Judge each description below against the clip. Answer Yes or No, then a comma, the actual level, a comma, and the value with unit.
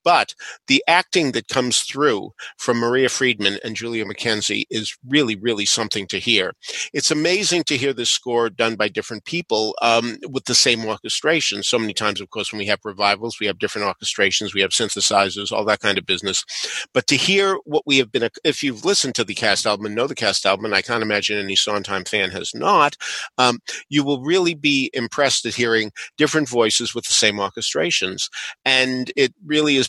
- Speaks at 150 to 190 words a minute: No, average, 200 wpm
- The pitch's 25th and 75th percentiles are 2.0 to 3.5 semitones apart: No, average, 4.6 semitones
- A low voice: Yes, low, 115 Hz